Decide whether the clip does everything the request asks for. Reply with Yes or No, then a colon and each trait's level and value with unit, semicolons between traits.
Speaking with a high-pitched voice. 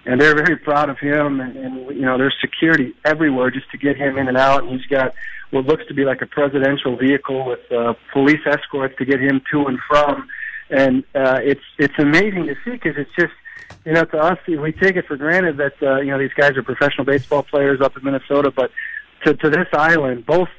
No: medium, 140 Hz